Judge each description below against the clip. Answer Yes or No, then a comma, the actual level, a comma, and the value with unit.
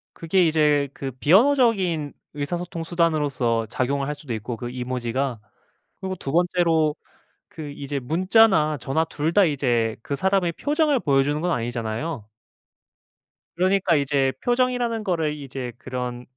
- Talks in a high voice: No, medium, 150 Hz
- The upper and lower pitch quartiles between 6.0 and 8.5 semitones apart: No, average, 5.3 semitones